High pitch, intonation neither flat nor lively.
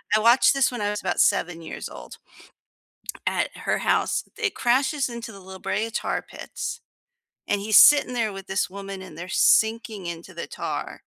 Yes: high, 210 Hz; average, 4.1 semitones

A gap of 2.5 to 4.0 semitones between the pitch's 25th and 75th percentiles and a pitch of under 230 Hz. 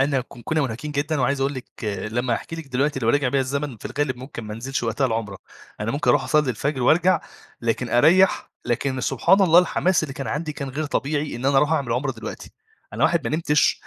Yes: average, 3.6 semitones; medium, 140 Hz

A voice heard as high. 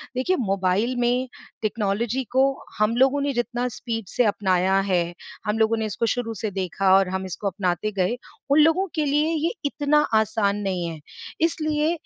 Yes: high, 225 Hz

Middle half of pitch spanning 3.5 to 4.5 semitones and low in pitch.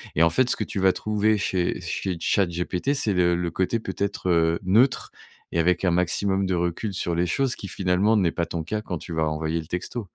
No: average, 3.1 semitones; very low, 90 Hz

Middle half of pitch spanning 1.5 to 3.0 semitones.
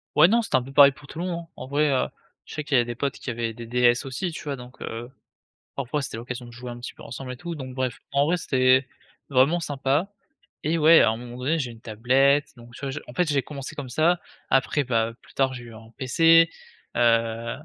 No: average, 3.5 semitones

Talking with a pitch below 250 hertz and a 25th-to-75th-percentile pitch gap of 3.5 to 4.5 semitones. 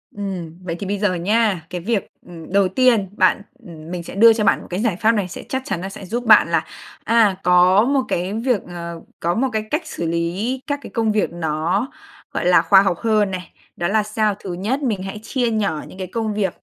Yes: high, 195 Hz; average, 4.0 semitones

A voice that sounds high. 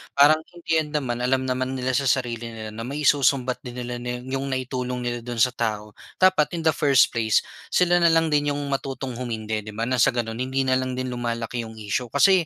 No: low, 125 Hz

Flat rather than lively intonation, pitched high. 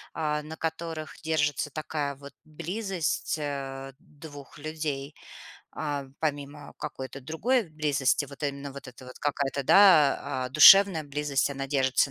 No: narrow, 2.1 semitones; medium, 145 Hz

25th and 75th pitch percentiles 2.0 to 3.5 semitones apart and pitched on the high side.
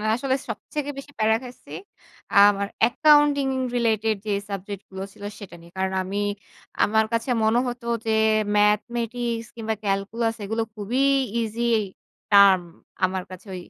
Yes: average, 3.2 semitones; high, 220 Hz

